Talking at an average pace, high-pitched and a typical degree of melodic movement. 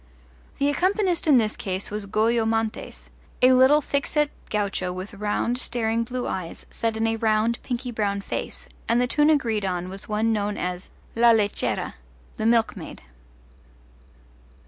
Yes: average, 155 wpm; high, 225 Hz; average, 3.2 semitones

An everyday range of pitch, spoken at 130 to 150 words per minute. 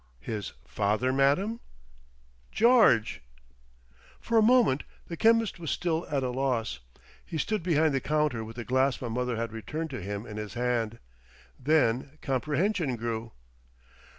No: wide, 5.8 semitones; average, 145 wpm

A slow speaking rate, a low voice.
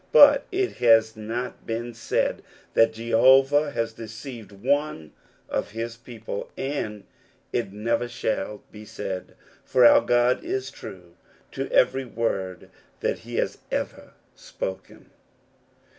Yes: slow, 115 wpm; low, 115 Hz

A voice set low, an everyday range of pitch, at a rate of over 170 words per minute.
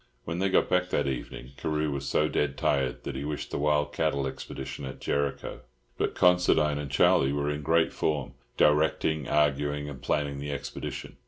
No: very low, 75 Hz; narrow, 1.6 semitones; average, 180 wpm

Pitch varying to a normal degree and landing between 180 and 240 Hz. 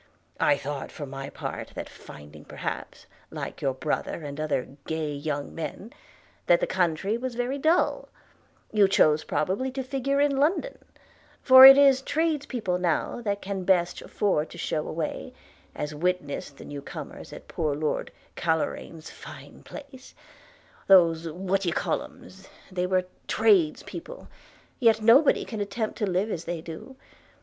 No: wide, 8.6 semitones; medium, 185 Hz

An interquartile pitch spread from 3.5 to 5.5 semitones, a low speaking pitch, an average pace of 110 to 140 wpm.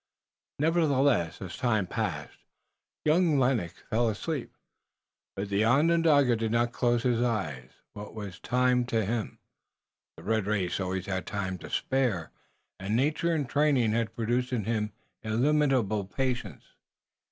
Yes: average, 4.6 semitones; low, 115 Hz; slow, 135 wpm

